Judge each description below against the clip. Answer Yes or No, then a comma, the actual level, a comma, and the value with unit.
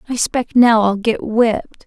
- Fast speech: No, average, 195 wpm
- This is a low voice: No, high, 225 Hz